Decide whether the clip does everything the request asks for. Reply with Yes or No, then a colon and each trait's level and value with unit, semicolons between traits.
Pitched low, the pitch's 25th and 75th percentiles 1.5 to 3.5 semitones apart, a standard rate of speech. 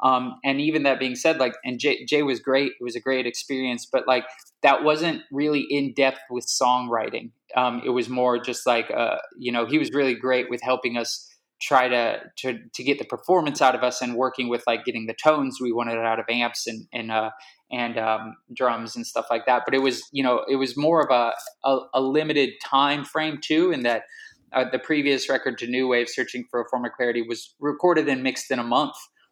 No: low, 130 Hz; narrow, 2.6 semitones; fast, 225 wpm